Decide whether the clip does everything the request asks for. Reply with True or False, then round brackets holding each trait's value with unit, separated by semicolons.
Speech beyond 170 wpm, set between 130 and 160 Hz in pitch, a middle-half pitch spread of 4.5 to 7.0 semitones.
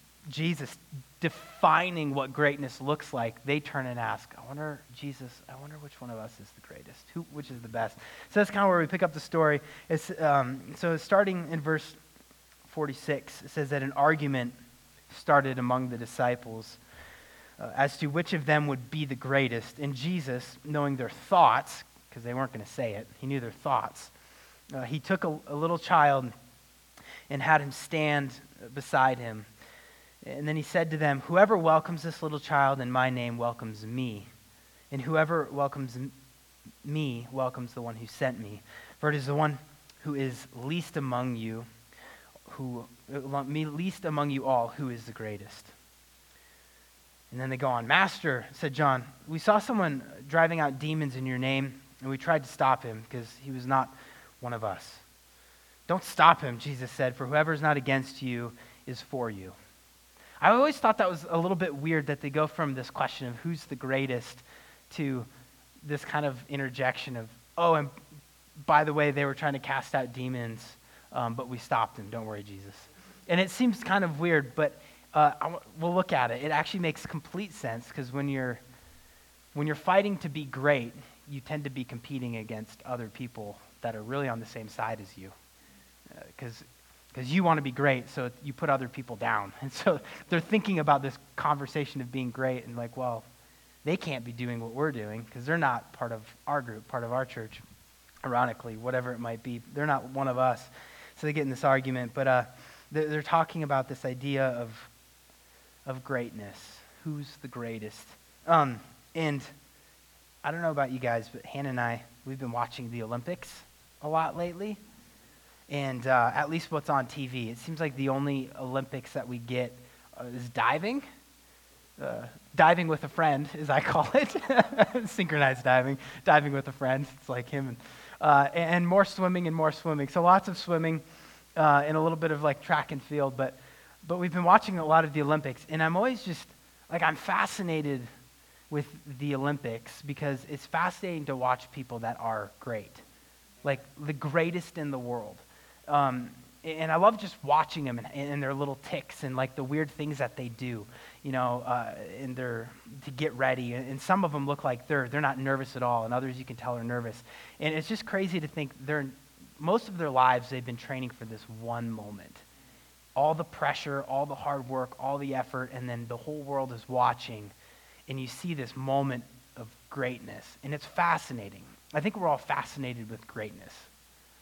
False (190 wpm; 135 Hz; 3.9 semitones)